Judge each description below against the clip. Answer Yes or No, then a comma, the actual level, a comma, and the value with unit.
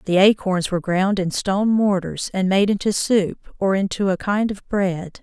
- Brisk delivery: No, average, 195 wpm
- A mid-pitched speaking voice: No, high, 195 Hz